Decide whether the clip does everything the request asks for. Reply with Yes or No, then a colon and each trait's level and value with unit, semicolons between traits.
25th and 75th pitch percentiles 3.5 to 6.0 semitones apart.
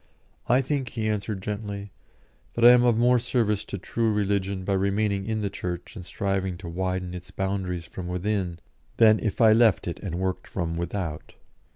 No: average, 3.0 semitones